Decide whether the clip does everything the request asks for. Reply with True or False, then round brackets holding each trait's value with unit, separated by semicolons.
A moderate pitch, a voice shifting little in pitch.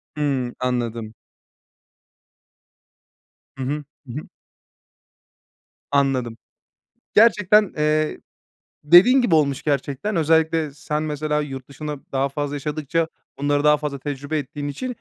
True (150 Hz; 2.3 semitones)